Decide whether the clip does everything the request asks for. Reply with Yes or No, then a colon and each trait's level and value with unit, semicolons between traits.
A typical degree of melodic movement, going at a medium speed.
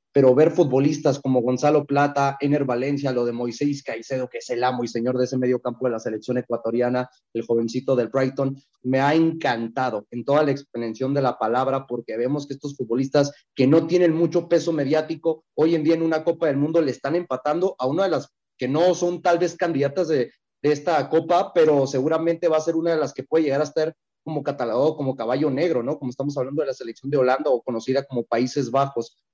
No: average, 3.8 semitones; fast, 220 wpm